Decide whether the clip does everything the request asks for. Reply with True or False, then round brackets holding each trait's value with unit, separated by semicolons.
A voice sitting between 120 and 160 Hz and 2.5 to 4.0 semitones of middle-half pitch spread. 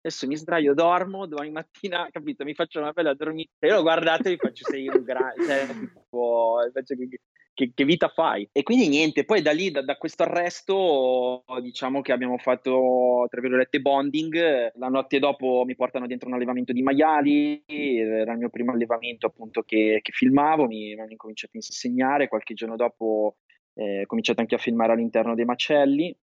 False (135 Hz; 4.5 semitones)